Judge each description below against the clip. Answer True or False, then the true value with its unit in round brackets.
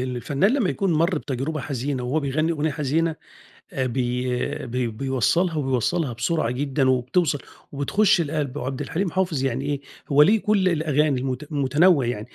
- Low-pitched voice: False (145 Hz)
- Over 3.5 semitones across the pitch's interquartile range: True (4.1 semitones)